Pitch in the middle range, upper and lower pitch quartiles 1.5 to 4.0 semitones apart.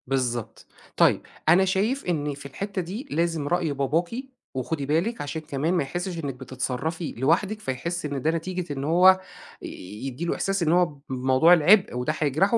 No: medium, 160 Hz; average, 4.6 semitones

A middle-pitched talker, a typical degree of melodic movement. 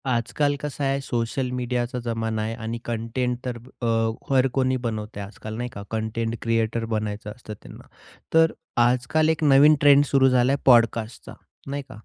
No: low, 120 Hz; average, 3.0 semitones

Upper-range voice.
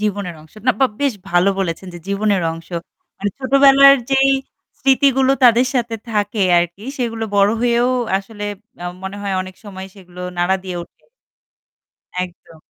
Yes: high, 205 Hz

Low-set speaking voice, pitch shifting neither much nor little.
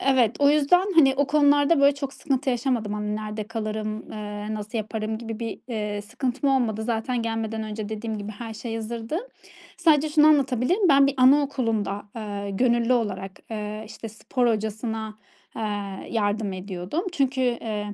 No: high, 225 Hz; average, 4.0 semitones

